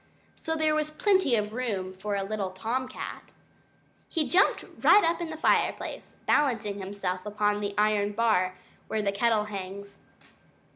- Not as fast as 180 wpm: Yes, average, 155 wpm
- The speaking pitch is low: No, high, 210 Hz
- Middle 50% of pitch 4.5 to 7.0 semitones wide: Yes, average, 4.9 semitones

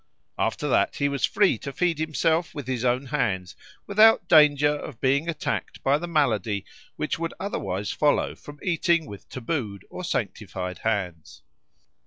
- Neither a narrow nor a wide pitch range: No, wide, 6.2 semitones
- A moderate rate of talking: Yes, average, 155 wpm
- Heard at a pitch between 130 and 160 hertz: Yes, medium, 140 Hz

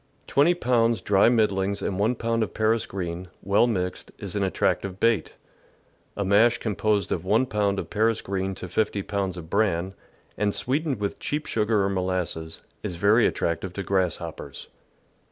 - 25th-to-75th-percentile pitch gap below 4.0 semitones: Yes, average, 3.1 semitones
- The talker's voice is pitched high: No, low, 100 Hz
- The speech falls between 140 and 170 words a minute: Yes, average, 165 wpm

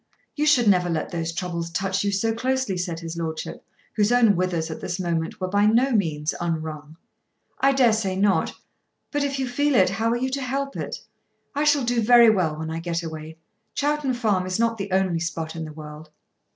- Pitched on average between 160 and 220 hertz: Yes, high, 190 Hz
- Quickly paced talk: Yes, fast, 210 wpm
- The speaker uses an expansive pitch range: Yes, wide, 6.5 semitones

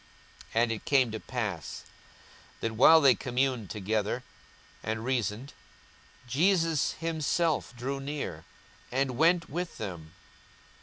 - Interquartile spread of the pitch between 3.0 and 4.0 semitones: No, average, 5.2 semitones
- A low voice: Yes, low, 130 Hz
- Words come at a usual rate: No, slow, 115 wpm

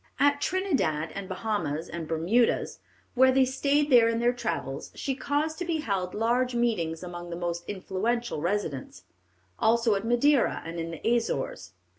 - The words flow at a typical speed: Yes, average, 160 wpm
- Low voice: No, high, 225 Hz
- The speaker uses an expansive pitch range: Yes, wide, 6.9 semitones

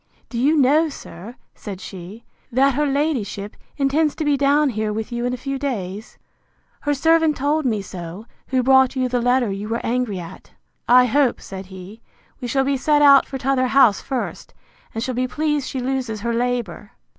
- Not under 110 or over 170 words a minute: No, average, 190 wpm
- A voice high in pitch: Yes, very high, 250 Hz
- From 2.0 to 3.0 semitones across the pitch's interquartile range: No, average, 4.2 semitones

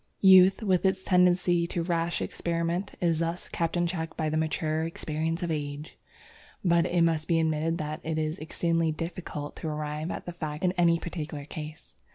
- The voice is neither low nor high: Yes, medium, 165 Hz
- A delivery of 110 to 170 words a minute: No, average, 185 wpm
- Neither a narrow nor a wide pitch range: No, narrow, 2.0 semitones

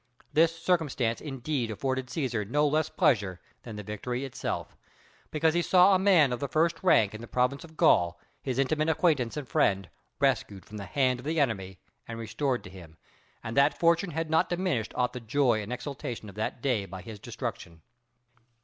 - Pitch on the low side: Yes, low, 130 Hz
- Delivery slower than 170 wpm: No, average, 195 wpm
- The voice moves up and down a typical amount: No, wide, 6.2 semitones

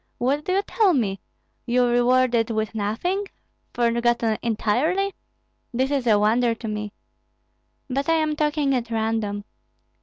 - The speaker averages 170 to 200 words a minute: No, average, 140 wpm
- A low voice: No, high, 240 Hz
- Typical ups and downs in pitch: Yes, average, 4.4 semitones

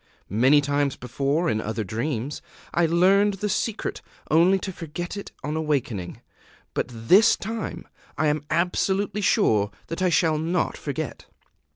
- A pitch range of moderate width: Yes, average, 5.0 semitones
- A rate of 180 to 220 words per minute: No, average, 145 wpm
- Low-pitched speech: No, medium, 160 Hz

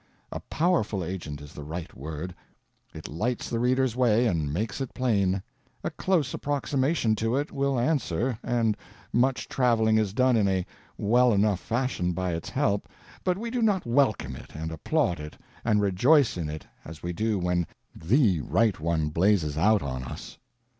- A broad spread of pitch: Yes, wide, 6.8 semitones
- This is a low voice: Yes, low, 105 Hz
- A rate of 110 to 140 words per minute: No, average, 175 wpm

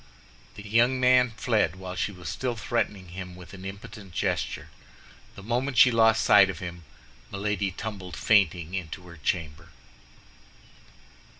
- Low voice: Yes, low, 100 Hz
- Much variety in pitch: No, average, 3.9 semitones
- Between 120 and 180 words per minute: Yes, average, 140 wpm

